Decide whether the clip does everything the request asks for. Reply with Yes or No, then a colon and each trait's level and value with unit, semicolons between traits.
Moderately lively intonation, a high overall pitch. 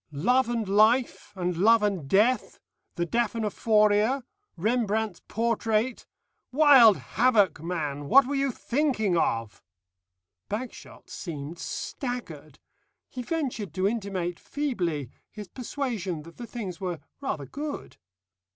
No: wide, 5.7 semitones; high, 215 Hz